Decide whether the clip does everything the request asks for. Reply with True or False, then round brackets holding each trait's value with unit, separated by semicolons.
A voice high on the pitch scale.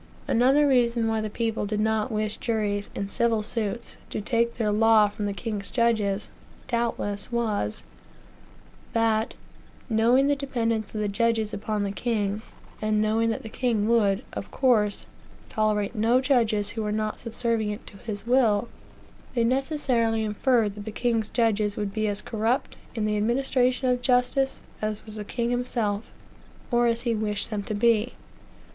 True (220 Hz)